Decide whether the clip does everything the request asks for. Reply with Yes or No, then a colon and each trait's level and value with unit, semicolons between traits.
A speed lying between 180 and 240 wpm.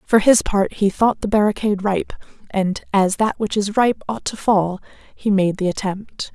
Yes: average, 200 wpm